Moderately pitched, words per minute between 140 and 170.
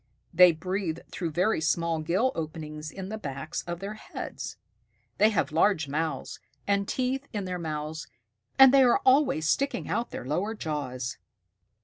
Yes: medium, 175 Hz; average, 155 wpm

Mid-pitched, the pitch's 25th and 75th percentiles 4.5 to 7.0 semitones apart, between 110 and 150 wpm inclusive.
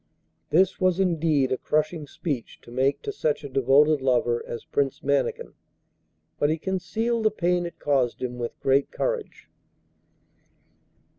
Yes: medium, 150 Hz; average, 5.1 semitones; average, 145 wpm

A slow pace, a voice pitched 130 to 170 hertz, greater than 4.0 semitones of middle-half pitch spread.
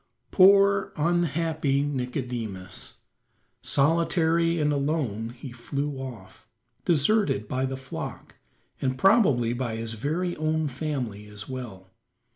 Yes: slow, 105 wpm; medium, 140 Hz; average, 5.3 semitones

